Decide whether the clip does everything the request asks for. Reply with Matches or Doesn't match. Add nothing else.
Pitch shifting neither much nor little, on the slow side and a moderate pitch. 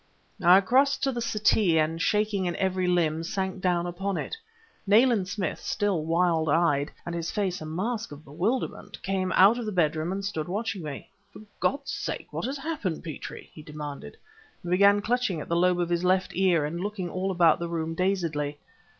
Doesn't match